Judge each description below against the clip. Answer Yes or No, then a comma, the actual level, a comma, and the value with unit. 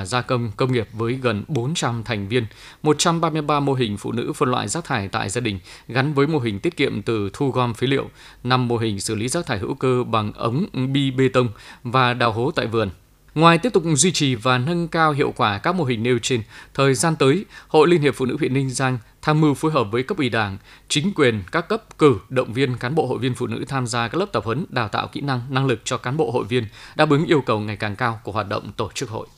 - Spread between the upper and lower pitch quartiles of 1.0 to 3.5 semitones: No, average, 4.3 semitones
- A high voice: No, low, 130 Hz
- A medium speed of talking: No, fast, 260 wpm